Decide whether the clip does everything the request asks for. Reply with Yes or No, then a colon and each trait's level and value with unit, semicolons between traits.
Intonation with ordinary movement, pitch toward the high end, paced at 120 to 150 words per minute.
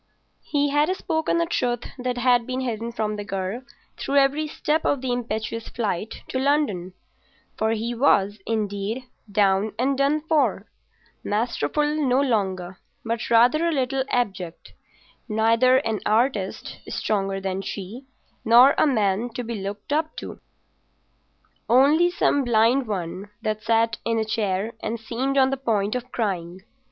Yes: average, 4.5 semitones; high, 230 Hz; average, 145 wpm